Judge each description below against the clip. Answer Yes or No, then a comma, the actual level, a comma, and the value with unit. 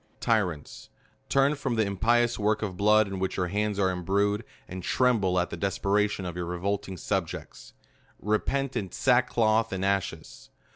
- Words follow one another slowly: No, average, 160 wpm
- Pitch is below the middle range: Yes, low, 100 Hz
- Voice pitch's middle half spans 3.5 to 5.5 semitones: No, average, 3.0 semitones